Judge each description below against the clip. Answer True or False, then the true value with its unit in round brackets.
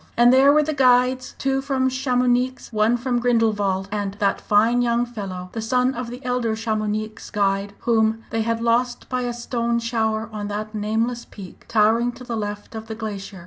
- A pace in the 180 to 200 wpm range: True (185 wpm)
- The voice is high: True (230 Hz)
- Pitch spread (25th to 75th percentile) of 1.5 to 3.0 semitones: True (2.5 semitones)